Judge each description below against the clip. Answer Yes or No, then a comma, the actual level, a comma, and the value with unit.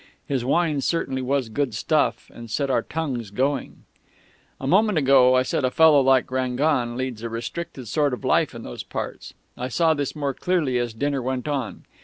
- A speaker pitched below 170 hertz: Yes, low, 135 Hz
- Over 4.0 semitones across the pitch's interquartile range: No, average, 2.9 semitones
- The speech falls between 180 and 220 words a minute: Yes, average, 190 wpm